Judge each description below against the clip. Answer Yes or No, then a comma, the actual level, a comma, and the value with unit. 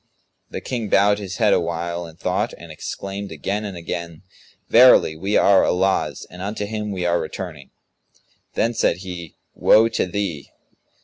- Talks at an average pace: Yes, average, 160 wpm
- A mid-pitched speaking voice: No, very low, 95 Hz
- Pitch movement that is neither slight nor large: Yes, average, 3.2 semitones